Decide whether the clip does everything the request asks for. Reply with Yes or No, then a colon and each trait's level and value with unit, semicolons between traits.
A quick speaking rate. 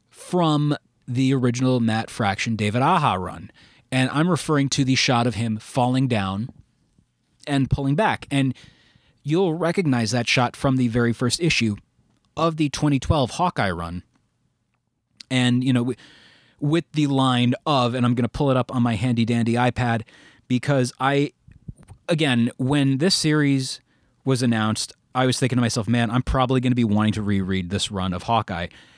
No: average, 170 wpm